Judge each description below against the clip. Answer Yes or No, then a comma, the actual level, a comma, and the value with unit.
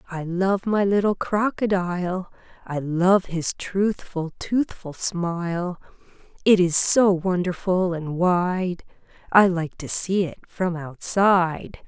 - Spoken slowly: Yes, slow, 115 wpm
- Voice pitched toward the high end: No, medium, 180 Hz